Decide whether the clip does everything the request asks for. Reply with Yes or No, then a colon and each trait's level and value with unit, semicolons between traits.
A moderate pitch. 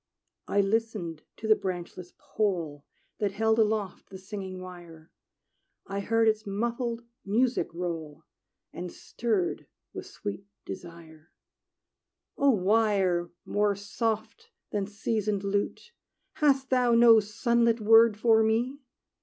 No: high, 210 Hz